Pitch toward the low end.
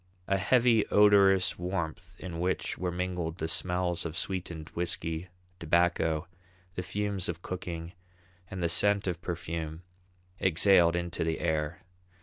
Yes: very low, 90 Hz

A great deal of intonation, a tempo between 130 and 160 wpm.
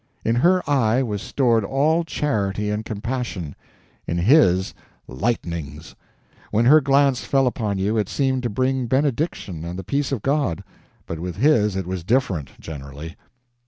Yes: wide, 6.6 semitones; average, 155 wpm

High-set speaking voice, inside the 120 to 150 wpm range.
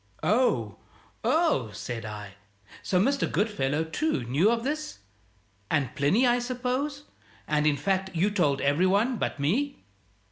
Yes: high, 195 Hz; average, 140 wpm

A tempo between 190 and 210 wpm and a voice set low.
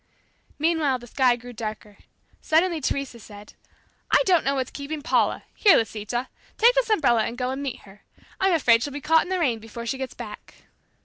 No: average, 195 wpm; very high, 265 Hz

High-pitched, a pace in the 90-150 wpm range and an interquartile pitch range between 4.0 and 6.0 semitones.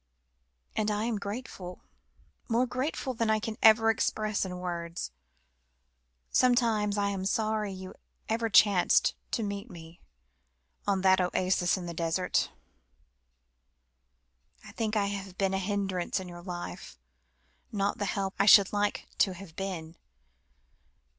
No: high, 200 Hz; slow, 135 wpm; average, 2.9 semitones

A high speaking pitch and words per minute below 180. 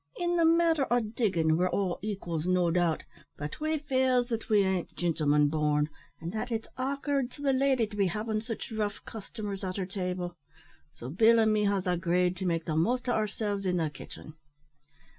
No: high, 200 Hz; average, 195 wpm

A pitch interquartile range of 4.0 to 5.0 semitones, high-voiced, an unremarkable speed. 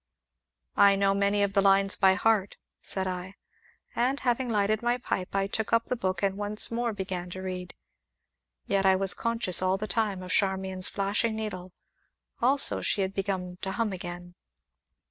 No: narrow, 2.5 semitones; high, 195 Hz; average, 175 wpm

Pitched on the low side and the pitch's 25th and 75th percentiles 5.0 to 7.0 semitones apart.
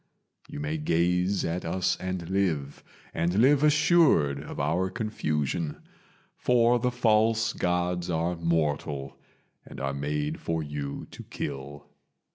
Yes: very low, 85 Hz; wide, 5.4 semitones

